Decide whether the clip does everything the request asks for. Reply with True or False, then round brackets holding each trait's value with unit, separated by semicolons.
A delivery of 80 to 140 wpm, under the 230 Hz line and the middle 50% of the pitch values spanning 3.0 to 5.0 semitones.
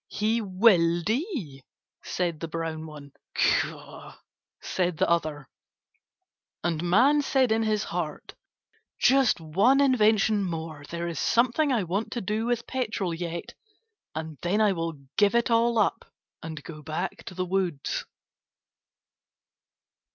False (135 wpm; 185 Hz; 5.6 semitones)